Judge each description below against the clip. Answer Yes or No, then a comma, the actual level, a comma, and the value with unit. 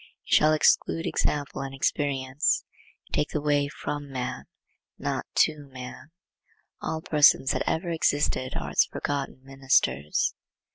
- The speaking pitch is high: No, medium, 140 Hz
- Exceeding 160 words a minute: No, slow, 135 wpm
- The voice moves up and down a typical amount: No, narrow, 2.1 semitones